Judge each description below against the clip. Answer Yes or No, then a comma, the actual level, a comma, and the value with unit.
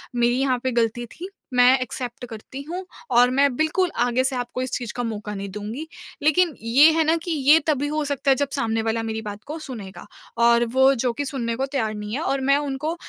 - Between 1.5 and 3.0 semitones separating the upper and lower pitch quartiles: No, average, 3.7 semitones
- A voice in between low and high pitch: No, very high, 255 Hz